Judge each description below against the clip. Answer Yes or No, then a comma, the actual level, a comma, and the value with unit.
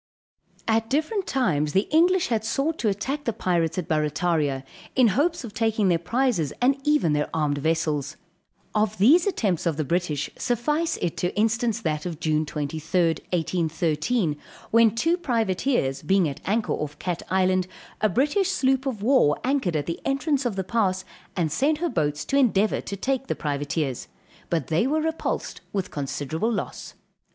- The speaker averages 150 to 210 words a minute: Yes, average, 170 wpm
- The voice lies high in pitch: Yes, high, 195 Hz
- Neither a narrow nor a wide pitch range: No, wide, 8.4 semitones